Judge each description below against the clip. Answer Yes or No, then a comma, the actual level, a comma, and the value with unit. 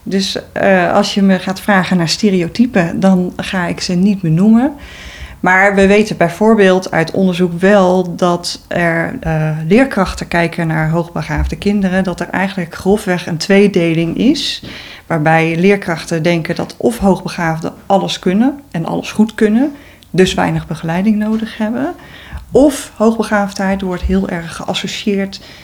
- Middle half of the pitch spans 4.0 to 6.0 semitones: No, average, 3.1 semitones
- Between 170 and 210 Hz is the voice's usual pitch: Yes, high, 190 Hz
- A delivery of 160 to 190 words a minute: No, average, 145 wpm